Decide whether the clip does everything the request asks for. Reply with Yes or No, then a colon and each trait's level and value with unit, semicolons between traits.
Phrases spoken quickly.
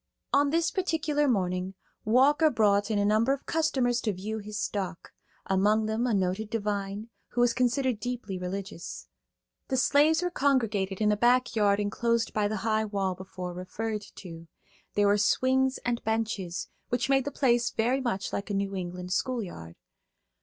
No: average, 165 wpm